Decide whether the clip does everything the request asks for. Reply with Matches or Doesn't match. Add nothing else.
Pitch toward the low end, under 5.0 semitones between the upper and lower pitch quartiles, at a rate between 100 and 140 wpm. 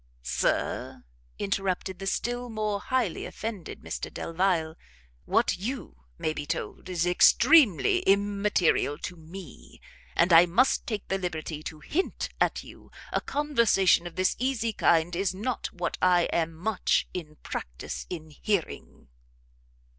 Doesn't match